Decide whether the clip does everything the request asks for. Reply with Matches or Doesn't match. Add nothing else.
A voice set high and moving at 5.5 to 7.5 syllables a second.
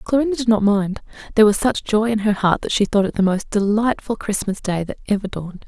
Matches